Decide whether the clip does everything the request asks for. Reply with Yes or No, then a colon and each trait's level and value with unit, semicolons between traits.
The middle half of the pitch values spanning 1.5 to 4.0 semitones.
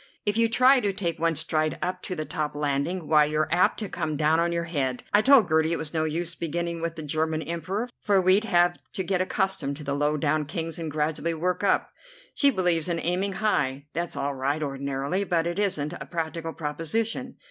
Yes: average, 3.2 semitones